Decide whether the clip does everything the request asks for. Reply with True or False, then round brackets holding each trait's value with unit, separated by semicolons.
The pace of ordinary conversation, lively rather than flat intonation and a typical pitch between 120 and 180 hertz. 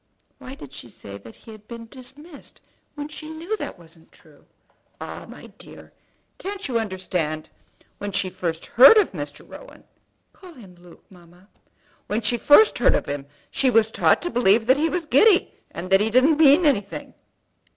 False (185 wpm; 8.7 semitones; 225 Hz)